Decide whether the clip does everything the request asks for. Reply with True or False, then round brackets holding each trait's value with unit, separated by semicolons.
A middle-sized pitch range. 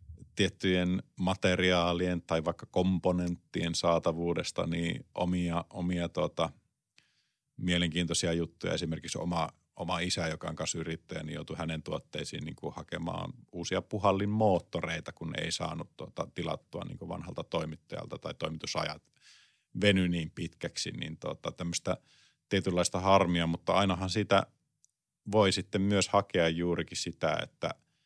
False (1.8 semitones)